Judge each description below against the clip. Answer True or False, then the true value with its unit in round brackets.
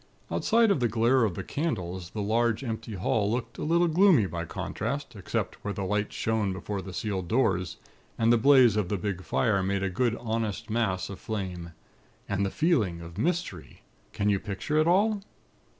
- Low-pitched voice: True (110 Hz)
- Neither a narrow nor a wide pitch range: True (4.7 semitones)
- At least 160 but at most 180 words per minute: False (190 wpm)